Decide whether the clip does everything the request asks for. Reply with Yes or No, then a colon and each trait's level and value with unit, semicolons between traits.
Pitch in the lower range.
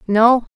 No: high, 230 Hz